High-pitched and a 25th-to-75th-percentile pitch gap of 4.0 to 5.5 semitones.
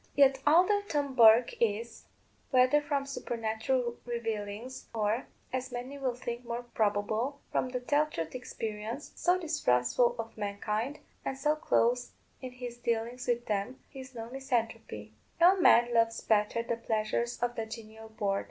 No: high, 240 Hz; average, 2.9 semitones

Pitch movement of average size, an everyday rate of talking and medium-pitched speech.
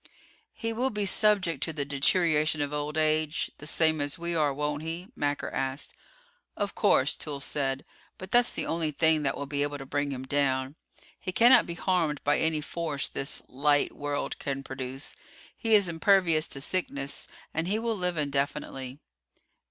Yes: average, 3.3 semitones; average, 175 wpm; medium, 150 Hz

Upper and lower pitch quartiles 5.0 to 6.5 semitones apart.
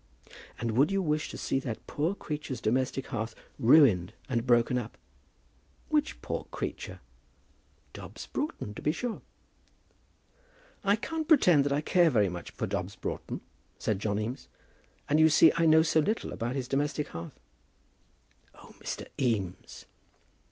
Yes: wide, 5.6 semitones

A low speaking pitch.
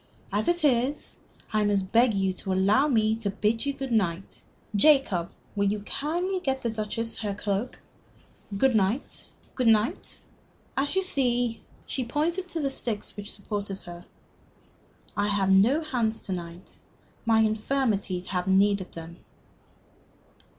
No: high, 220 Hz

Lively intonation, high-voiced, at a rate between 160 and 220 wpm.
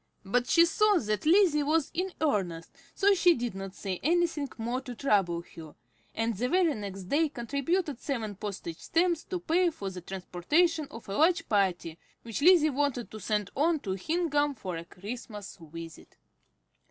Yes: wide, 8.9 semitones; high, 245 Hz; average, 170 wpm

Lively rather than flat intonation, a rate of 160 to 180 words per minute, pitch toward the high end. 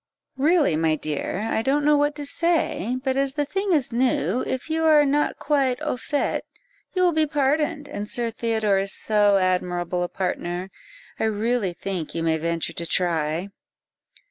Yes: wide, 8.2 semitones; average, 175 wpm; high, 230 Hz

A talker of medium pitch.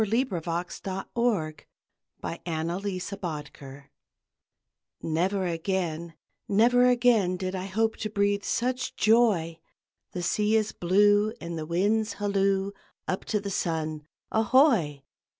No: high, 195 Hz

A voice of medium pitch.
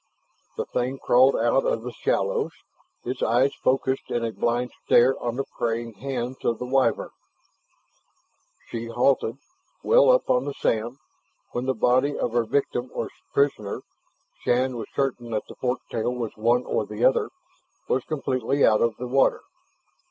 No: low, 125 Hz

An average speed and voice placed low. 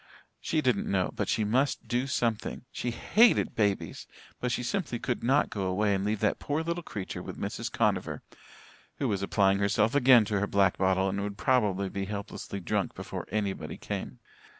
Yes: average, 185 wpm; low, 105 Hz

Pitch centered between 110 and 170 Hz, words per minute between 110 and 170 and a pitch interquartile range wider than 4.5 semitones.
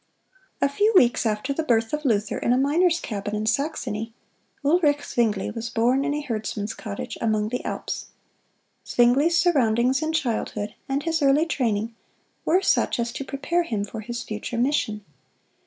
No: high, 245 Hz; average, 165 wpm; average, 5.1 semitones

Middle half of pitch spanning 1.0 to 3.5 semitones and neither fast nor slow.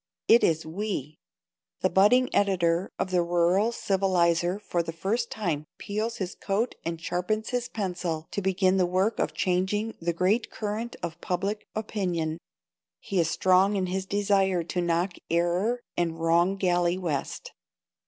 Yes: average, 3.1 semitones; average, 155 wpm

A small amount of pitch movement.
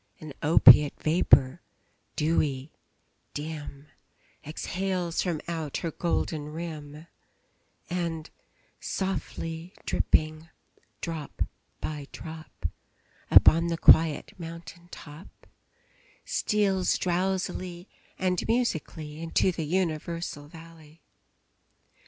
Yes: narrow, 2.3 semitones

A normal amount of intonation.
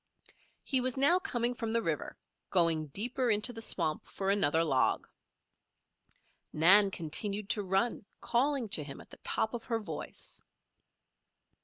No: wide, 6.2 semitones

